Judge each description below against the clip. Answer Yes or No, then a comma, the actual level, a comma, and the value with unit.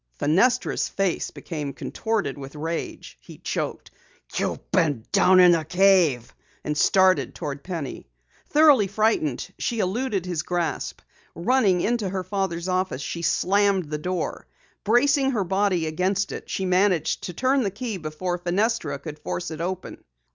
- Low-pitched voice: No, medium, 185 Hz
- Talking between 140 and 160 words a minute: Yes, average, 145 wpm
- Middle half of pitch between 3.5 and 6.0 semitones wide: Yes, average, 4.1 semitones